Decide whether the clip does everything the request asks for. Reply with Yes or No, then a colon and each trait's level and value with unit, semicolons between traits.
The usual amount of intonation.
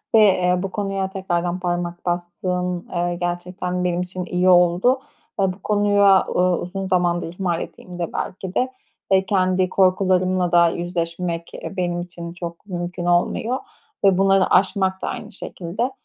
No: narrow, 1.5 semitones